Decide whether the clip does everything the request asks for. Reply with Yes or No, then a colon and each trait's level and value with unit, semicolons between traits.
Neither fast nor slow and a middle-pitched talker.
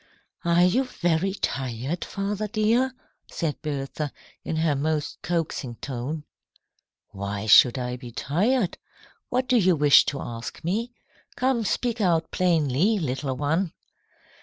No: slow, 130 wpm; medium, 160 Hz